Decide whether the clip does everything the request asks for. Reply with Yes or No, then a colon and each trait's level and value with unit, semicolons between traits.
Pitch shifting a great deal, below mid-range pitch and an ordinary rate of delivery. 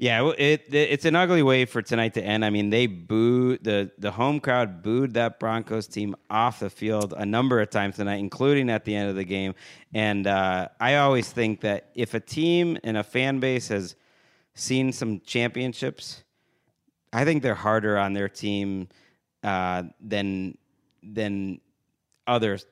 No: average, 3.9 semitones; low, 110 Hz; average, 175 wpm